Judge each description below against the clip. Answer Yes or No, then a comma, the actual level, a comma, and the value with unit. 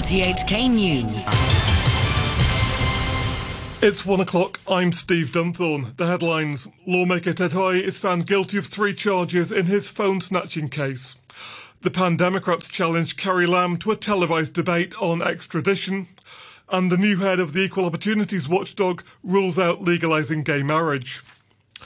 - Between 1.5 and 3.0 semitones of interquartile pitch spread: Yes, average, 2.7 semitones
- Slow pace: Yes, slow, 130 wpm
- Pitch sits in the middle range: Yes, medium, 180 Hz